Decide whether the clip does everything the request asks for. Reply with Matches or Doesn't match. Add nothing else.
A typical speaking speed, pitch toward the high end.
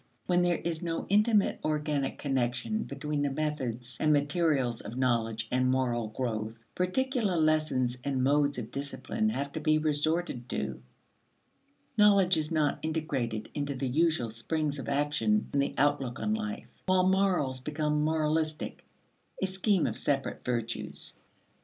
Doesn't match